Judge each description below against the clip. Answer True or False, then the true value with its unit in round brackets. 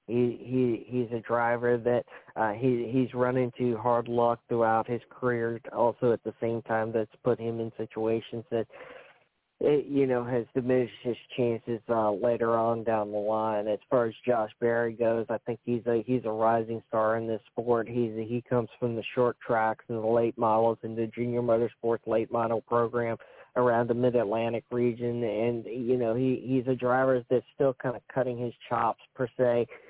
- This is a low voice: True (120 Hz)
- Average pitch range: False (1.3 semitones)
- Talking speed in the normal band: True (195 wpm)